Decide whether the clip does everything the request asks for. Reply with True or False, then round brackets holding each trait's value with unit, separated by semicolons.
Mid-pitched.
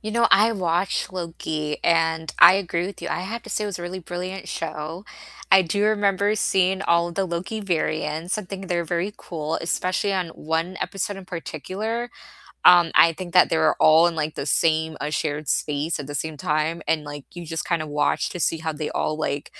True (170 Hz)